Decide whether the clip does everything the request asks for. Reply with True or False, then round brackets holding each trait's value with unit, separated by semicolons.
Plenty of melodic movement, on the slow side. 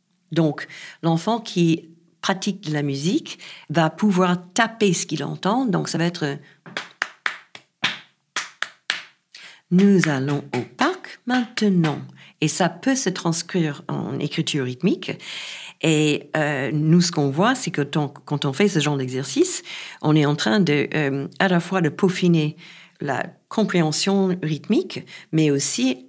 False (4.2 semitones; 140 wpm)